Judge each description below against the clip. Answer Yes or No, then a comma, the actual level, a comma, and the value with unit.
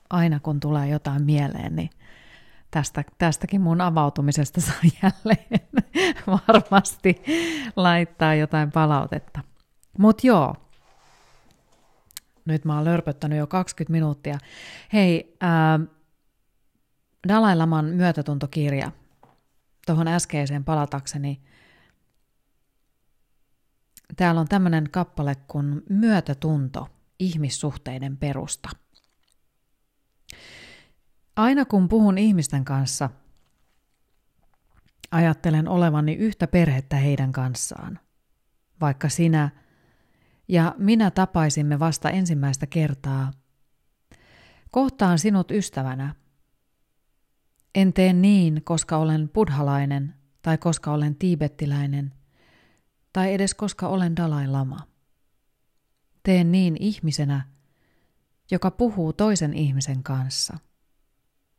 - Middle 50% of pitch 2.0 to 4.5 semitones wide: Yes, average, 4.2 semitones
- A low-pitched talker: No, medium, 155 Hz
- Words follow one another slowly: Yes, slow, 85 wpm